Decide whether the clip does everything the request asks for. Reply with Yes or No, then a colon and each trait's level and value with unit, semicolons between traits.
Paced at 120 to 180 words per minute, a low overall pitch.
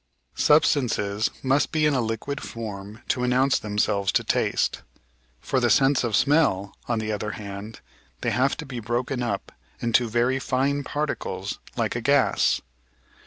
Yes: average, 155 wpm; low, 120 Hz